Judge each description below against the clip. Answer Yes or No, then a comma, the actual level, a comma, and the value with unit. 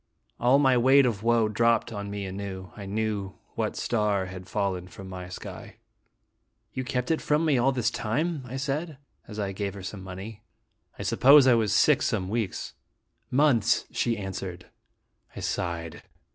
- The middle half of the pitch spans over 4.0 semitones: Yes, average, 4.7 semitones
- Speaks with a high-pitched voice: No, low, 110 Hz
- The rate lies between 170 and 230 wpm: Yes, average, 175 wpm